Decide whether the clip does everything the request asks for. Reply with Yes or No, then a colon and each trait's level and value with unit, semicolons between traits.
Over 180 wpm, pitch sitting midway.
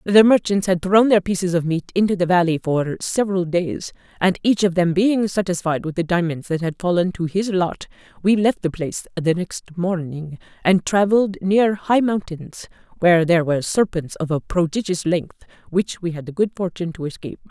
Yes: average, 195 wpm; medium, 180 Hz